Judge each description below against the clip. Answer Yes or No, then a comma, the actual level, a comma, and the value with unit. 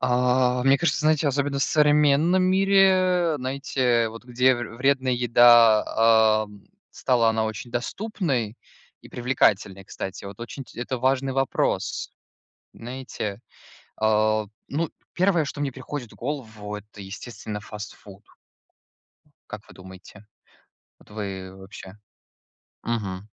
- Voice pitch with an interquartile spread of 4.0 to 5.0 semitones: Yes, average, 4.4 semitones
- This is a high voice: No, low, 120 Hz